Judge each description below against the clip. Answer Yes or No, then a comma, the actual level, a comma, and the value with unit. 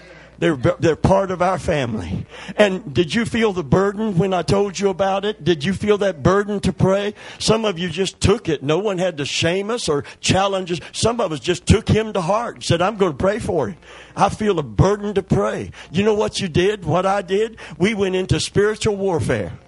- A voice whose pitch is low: No, high, 190 Hz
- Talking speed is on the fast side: Yes, fast, 230 wpm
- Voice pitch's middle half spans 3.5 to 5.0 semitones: No, average, 2.7 semitones